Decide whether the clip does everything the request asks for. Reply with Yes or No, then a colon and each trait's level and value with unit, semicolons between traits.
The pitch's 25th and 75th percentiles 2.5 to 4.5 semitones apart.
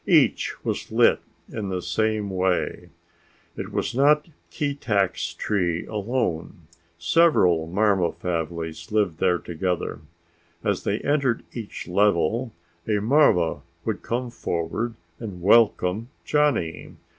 No: average, 5.1 semitones